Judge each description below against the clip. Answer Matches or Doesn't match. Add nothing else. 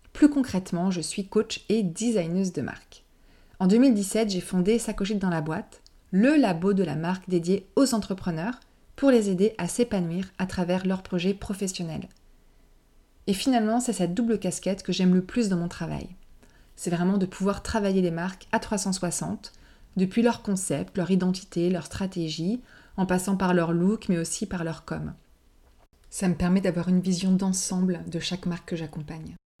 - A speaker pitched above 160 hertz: Matches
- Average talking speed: Matches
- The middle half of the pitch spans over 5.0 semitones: Doesn't match